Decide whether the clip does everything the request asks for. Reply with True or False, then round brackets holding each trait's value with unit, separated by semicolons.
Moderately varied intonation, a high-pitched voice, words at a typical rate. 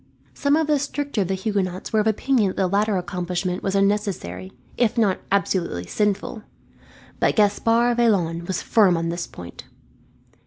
True (3.7 semitones; 200 Hz; 160 wpm)